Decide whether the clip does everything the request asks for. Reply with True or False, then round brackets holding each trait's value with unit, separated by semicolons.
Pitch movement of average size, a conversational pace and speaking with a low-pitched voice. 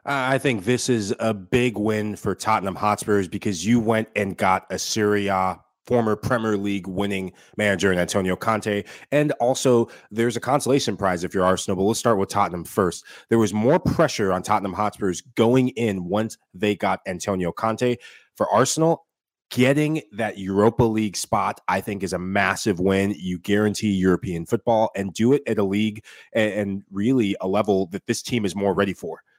True (3.1 semitones; 180 wpm; 105 Hz)